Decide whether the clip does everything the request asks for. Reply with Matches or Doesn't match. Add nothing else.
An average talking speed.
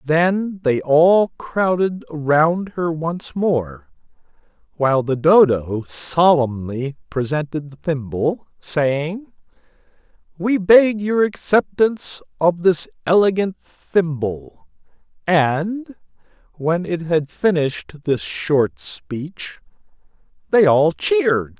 Doesn't match